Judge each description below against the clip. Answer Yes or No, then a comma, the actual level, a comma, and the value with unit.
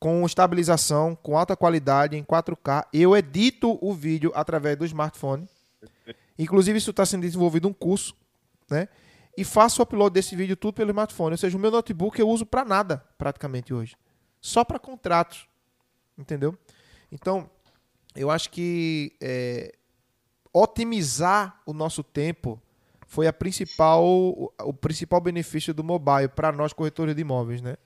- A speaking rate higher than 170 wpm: No, average, 150 wpm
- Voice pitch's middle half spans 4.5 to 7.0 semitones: Yes, average, 5.0 semitones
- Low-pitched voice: No, medium, 160 Hz